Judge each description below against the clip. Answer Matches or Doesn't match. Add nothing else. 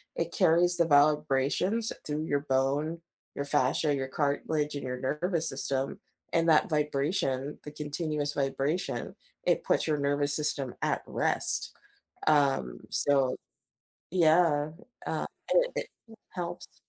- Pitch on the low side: Doesn't match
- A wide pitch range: Doesn't match